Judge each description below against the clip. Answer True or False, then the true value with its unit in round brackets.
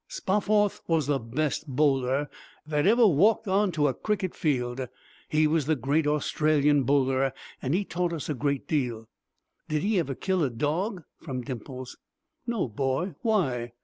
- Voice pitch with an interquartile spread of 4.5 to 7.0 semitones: True (5.3 semitones)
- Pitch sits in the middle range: True (150 Hz)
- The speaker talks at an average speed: True (160 wpm)